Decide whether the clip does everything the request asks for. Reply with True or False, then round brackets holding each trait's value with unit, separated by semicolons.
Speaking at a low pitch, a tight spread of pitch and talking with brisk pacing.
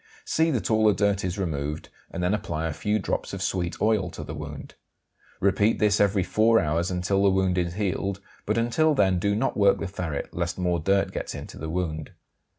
False (95 Hz; 3.3 semitones; 210 wpm)